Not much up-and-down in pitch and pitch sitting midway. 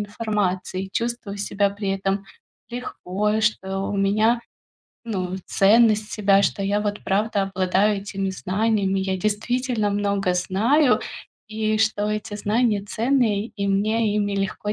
No: narrow, 1.9 semitones; high, 205 Hz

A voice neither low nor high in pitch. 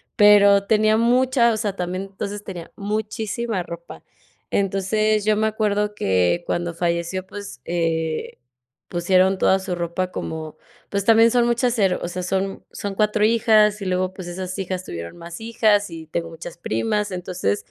No: high, 195 Hz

